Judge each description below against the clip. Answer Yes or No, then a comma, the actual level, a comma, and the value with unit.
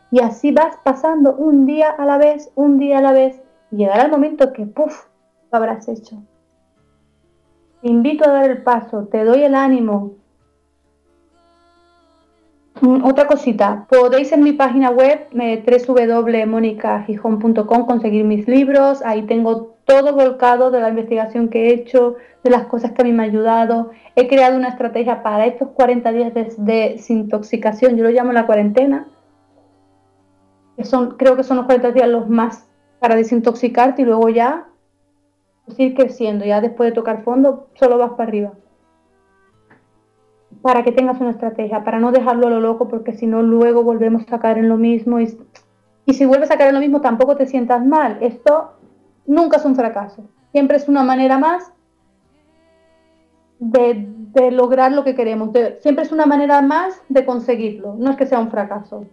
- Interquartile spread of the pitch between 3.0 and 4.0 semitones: Yes, average, 3.4 semitones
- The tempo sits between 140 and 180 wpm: Yes, average, 170 wpm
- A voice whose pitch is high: Yes, high, 240 Hz